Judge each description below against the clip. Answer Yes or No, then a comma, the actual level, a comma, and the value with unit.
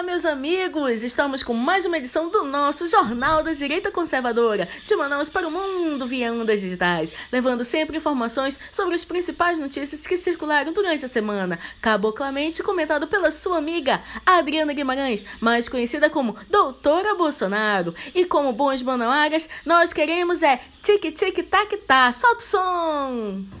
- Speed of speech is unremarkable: Yes, average, 155 wpm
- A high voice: Yes, very high, 300 Hz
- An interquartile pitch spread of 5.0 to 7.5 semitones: Yes, wide, 5.6 semitones